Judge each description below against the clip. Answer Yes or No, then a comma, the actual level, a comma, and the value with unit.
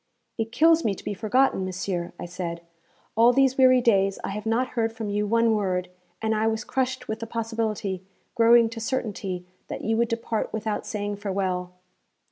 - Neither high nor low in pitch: No, high, 220 Hz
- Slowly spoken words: No, average, 185 wpm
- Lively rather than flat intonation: No, average, 3.0 semitones